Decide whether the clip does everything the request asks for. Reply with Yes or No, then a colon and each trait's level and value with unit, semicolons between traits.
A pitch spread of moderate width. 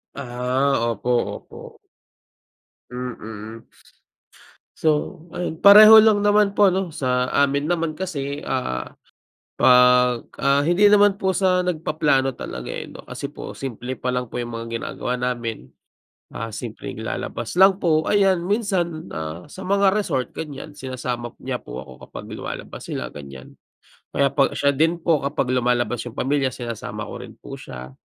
No: wide, 6.5 semitones